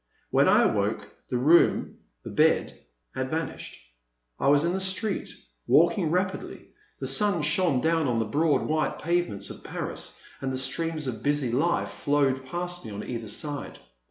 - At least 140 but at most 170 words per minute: Yes, average, 165 wpm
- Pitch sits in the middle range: Yes, medium, 150 Hz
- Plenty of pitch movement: No, average, 4.7 semitones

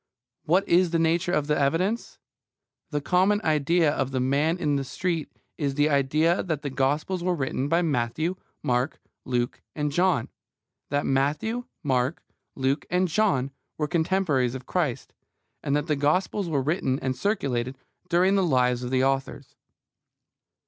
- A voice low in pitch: No, medium, 150 Hz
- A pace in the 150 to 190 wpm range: Yes, average, 155 wpm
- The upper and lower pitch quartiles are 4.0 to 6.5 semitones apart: Yes, average, 4.5 semitones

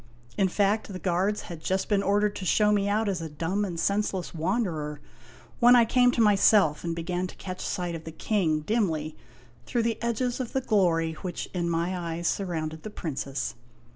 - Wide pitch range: No, average, 4.1 semitones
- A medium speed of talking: Yes, average, 195 wpm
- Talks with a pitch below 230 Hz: Yes, medium, 185 Hz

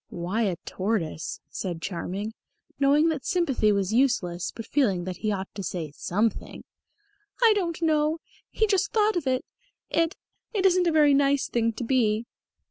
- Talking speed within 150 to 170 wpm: Yes, average, 165 wpm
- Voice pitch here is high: Yes, high, 245 Hz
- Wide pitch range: Yes, wide, 8.5 semitones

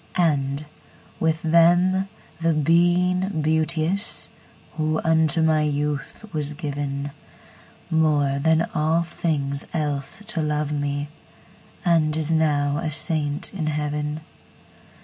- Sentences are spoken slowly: Yes, slow, 95 wpm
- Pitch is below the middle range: No, medium, 155 Hz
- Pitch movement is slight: Yes, narrow, 2.0 semitones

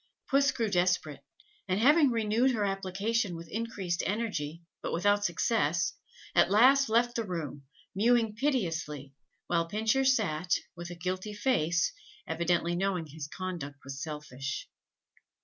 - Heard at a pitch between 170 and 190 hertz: Yes, medium, 185 Hz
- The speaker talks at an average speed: No, slow, 130 wpm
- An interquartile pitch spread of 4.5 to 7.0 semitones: Yes, average, 5.2 semitones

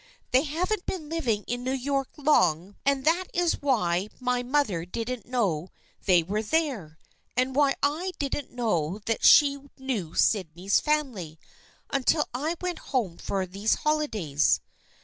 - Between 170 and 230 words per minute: No, average, 145 wpm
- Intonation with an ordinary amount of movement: No, wide, 7.2 semitones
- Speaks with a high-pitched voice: Yes, very high, 250 Hz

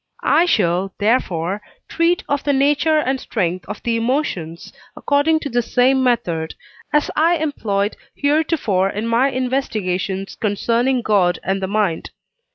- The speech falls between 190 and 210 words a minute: No, average, 140 wpm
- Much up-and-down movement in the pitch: Yes, wide, 6.6 semitones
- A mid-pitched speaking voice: No, high, 235 Hz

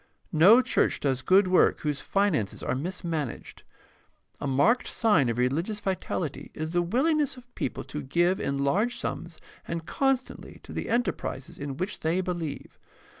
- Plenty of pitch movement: Yes, wide, 6.5 semitones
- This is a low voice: No, medium, 175 Hz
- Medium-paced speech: Yes, average, 155 wpm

